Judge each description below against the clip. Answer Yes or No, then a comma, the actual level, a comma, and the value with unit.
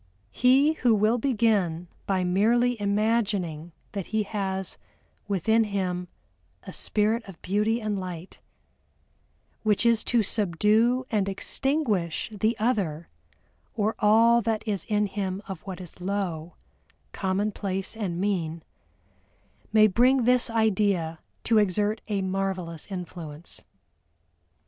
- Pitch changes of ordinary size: Yes, average, 3.2 semitones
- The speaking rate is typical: No, slow, 115 wpm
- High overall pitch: Yes, high, 205 Hz